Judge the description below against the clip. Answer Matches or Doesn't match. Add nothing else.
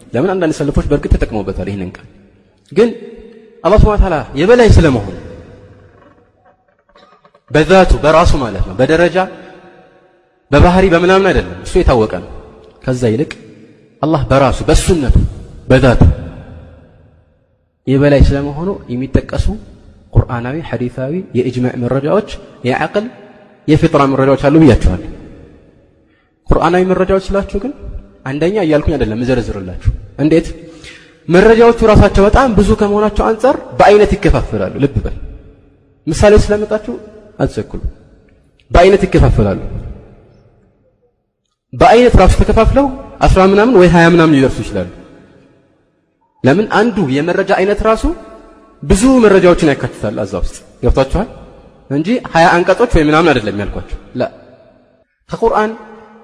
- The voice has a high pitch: Doesn't match